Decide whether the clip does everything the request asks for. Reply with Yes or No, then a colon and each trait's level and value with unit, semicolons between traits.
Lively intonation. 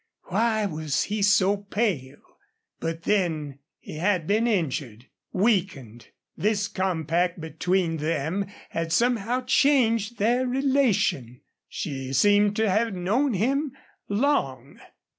Yes: wide, 5.7 semitones